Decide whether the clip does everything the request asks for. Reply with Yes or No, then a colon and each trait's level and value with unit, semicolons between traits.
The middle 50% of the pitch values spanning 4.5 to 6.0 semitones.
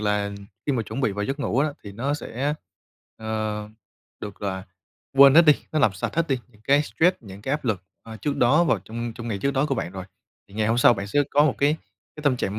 Yes: wide, 5.5 semitones